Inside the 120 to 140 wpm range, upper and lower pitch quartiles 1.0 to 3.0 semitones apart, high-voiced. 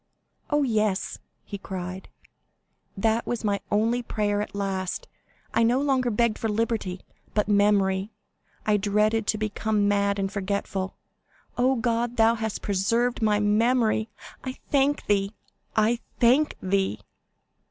Yes: slow, 135 wpm; narrow, 2.6 semitones; high, 215 Hz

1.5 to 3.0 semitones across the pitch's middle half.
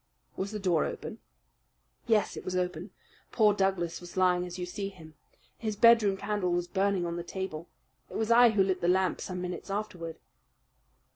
Yes: narrow, 2.4 semitones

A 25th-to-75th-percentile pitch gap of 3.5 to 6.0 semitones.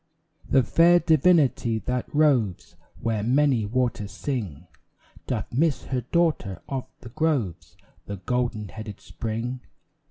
Yes: average, 5.0 semitones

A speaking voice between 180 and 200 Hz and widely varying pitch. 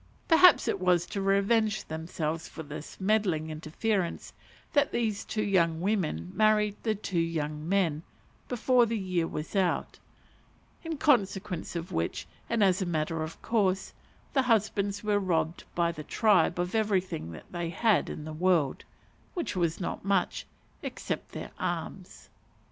No: medium, 185 Hz; average, 4.5 semitones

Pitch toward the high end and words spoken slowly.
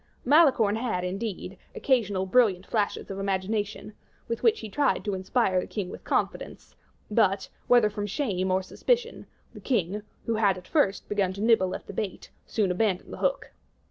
No: high, 205 Hz; average, 175 wpm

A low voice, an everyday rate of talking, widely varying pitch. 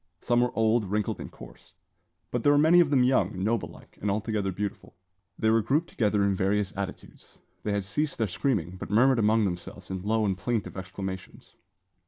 No: low, 105 Hz; average, 195 wpm; average, 3.7 semitones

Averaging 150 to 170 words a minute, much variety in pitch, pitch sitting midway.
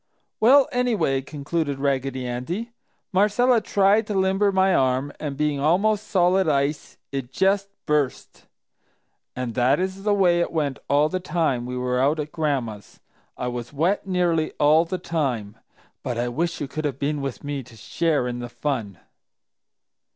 Yes: average, 165 wpm; wide, 6.1 semitones; medium, 150 Hz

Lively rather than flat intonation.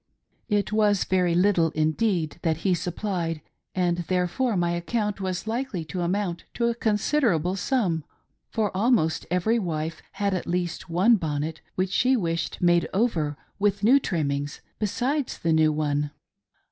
No: average, 4.2 semitones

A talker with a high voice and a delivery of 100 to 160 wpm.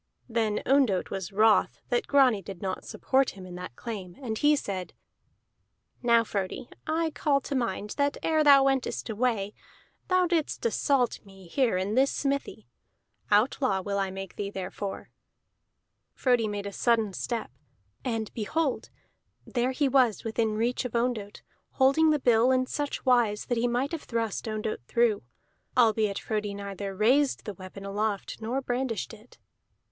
Yes: high, 230 Hz; average, 155 wpm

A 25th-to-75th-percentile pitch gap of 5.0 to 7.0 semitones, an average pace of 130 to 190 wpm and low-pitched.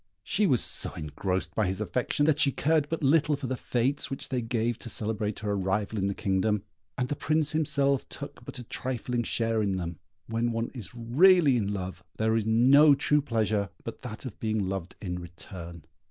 No: average, 5.3 semitones; average, 200 wpm; low, 115 Hz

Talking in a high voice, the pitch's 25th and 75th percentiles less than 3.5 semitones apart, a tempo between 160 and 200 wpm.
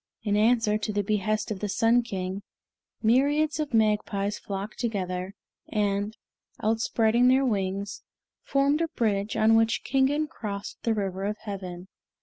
No: high, 215 Hz; average, 2.9 semitones; average, 140 wpm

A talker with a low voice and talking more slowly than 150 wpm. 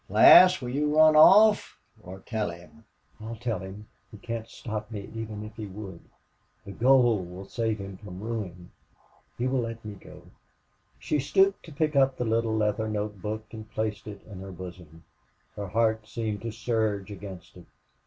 No: low, 110 Hz; average, 175 wpm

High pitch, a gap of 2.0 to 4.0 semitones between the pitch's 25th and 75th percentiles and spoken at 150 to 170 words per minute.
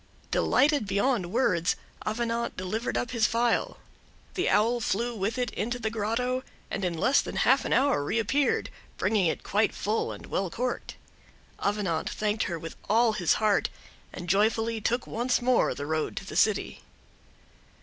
Yes: high, 220 Hz; average, 3.6 semitones; average, 160 wpm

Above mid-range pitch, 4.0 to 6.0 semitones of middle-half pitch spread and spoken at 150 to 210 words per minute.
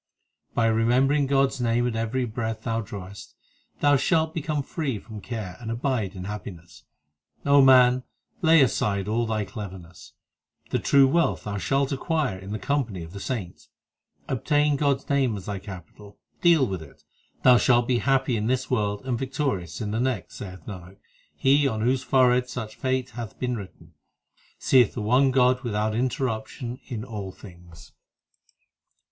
No: low, 120 Hz; average, 4.4 semitones; average, 170 wpm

